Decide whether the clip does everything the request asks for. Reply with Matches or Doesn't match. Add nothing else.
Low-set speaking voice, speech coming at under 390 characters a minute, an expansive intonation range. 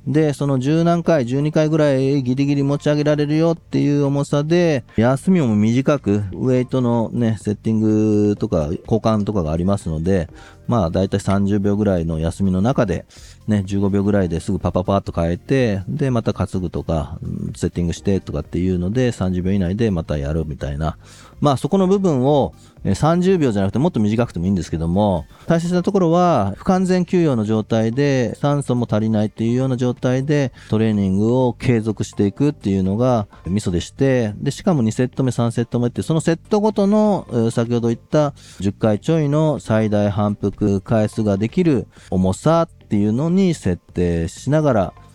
Matches